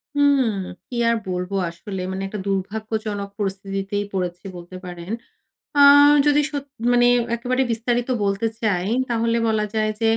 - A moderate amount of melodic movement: Yes, average, 3.3 semitones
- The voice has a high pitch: Yes, high, 210 Hz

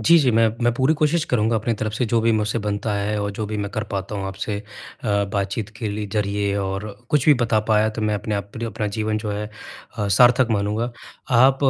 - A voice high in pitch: No, low, 110 Hz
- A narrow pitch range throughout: Yes, narrow, 2.3 semitones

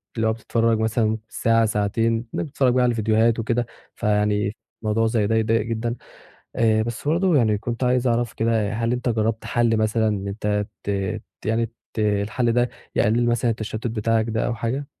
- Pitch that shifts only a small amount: Yes, narrow, 1.5 semitones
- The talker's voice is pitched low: Yes, low, 115 Hz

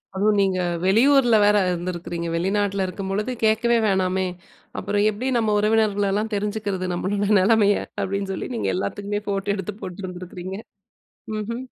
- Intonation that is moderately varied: No, narrow, 2.1 semitones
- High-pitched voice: Yes, high, 200 Hz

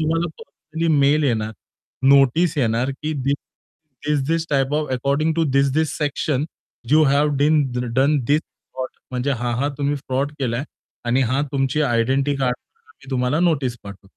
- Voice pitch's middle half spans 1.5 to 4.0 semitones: Yes, average, 2.8 semitones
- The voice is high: No, medium, 140 Hz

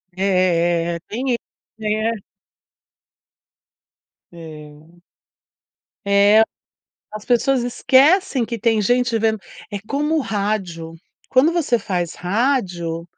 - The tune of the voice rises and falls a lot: Yes, wide, 6.0 semitones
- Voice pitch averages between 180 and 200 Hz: No, high, 215 Hz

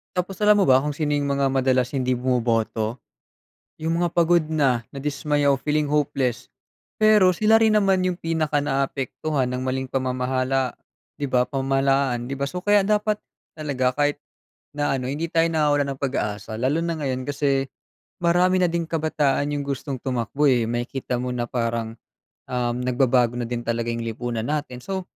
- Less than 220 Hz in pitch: Yes, low, 135 Hz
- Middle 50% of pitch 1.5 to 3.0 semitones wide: No, average, 3.7 semitones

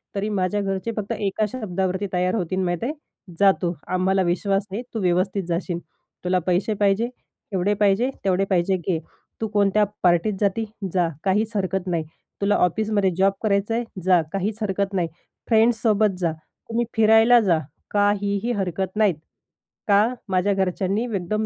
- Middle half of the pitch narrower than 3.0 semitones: Yes, narrow, 2.5 semitones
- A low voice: No, high, 195 Hz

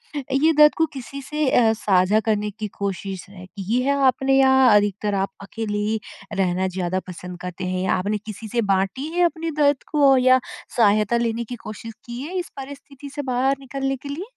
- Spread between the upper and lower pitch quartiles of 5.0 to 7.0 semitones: Yes, wide, 5.4 semitones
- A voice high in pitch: Yes, high, 230 Hz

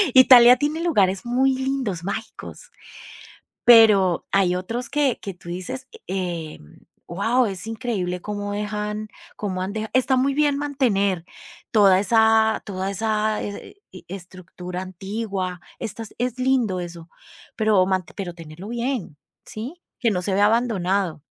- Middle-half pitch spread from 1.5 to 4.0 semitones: No, average, 4.5 semitones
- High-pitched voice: Yes, high, 210 Hz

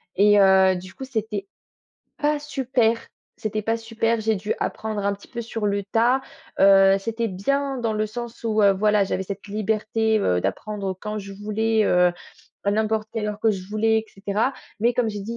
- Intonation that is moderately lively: No, narrow, 2.2 semitones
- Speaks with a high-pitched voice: Yes, high, 215 Hz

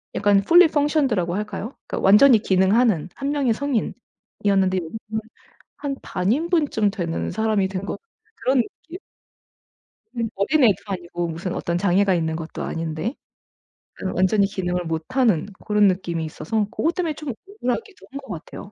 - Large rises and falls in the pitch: Yes, wide, 6.5 semitones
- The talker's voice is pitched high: Yes, high, 205 Hz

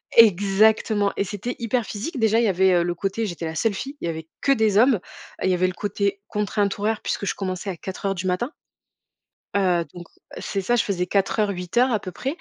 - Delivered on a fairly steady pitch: No, average, 3.1 semitones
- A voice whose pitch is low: No, high, 200 Hz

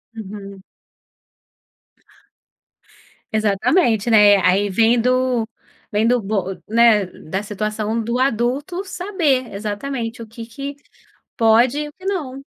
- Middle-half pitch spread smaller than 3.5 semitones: No, average, 3.8 semitones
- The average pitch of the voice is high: Yes, high, 230 Hz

